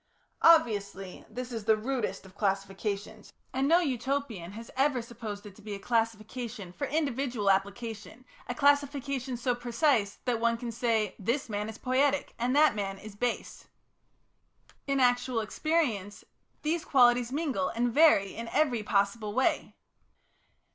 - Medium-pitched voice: No, high, 235 Hz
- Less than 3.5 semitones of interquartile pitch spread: No, average, 4.3 semitones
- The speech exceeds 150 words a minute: No, average, 145 wpm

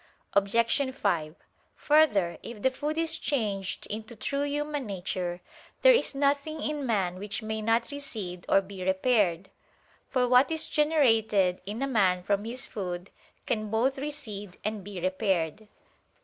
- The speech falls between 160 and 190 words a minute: No, average, 150 wpm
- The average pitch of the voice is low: No, high, 220 Hz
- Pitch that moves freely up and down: Yes, wide, 6.2 semitones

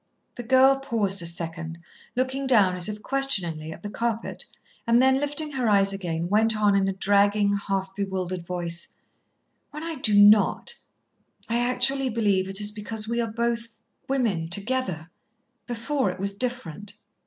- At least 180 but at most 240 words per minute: No, average, 160 wpm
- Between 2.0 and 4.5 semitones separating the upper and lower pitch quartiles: Yes, average, 4.2 semitones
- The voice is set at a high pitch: Yes, high, 210 Hz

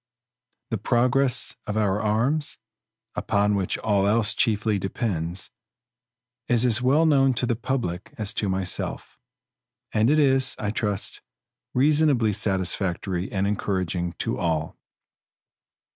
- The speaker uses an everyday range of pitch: Yes, average, 4.5 semitones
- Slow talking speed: Yes, slow, 120 wpm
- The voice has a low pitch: Yes, low, 105 Hz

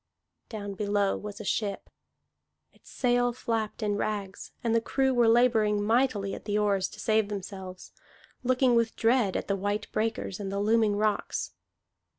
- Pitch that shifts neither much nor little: No, narrow, 2.2 semitones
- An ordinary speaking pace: Yes, average, 160 wpm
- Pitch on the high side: Yes, high, 215 Hz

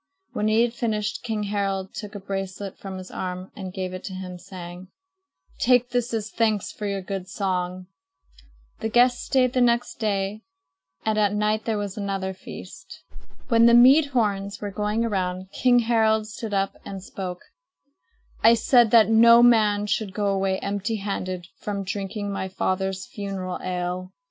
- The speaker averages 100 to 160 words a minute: No, average, 170 wpm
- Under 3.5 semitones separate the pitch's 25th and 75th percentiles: Yes, average, 2.8 semitones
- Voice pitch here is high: Yes, high, 205 Hz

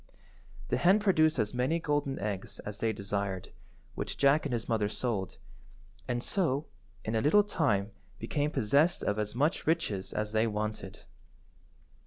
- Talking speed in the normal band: Yes, average, 155 wpm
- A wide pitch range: Yes, wide, 6.2 semitones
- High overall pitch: No, low, 120 Hz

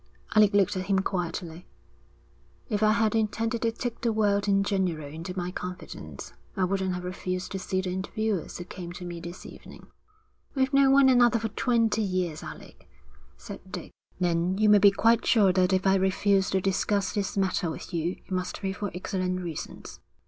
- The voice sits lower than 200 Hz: Yes, high, 190 Hz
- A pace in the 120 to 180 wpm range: No, average, 190 wpm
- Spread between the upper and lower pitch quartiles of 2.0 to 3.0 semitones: Yes, average, 2.7 semitones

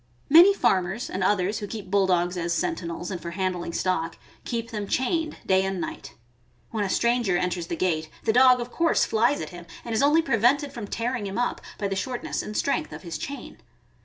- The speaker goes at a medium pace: No, fast, 215 wpm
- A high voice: Yes, high, 205 Hz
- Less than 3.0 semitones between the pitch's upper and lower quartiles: No, average, 5.2 semitones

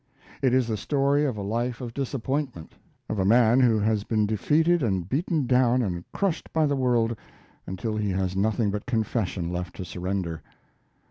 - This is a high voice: No, low, 115 Hz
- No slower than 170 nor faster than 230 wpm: Yes, average, 180 wpm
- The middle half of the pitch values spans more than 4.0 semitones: Yes, average, 4.8 semitones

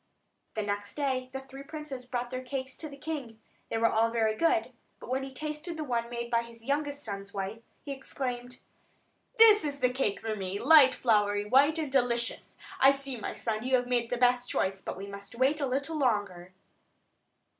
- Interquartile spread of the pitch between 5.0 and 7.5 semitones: No, average, 3.7 semitones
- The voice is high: Yes, very high, 250 Hz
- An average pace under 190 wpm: No, average, 200 wpm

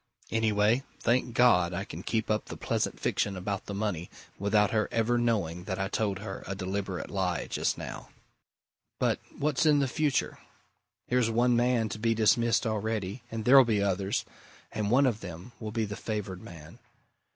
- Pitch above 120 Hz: No, low, 110 Hz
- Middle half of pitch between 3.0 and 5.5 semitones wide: Yes, average, 3.3 semitones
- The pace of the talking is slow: No, average, 175 wpm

